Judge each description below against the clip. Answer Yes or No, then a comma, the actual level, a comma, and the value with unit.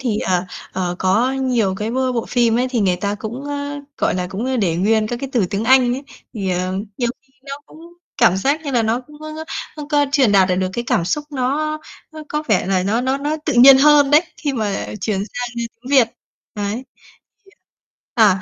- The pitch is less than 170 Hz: No, high, 245 Hz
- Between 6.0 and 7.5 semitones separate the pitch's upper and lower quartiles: No, wide, 5.6 semitones